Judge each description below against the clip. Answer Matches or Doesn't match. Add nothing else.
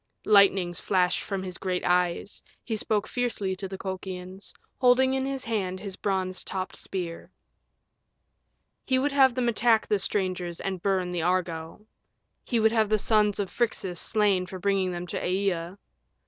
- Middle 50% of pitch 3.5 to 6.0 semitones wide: Doesn't match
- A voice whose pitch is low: Doesn't match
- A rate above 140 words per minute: Matches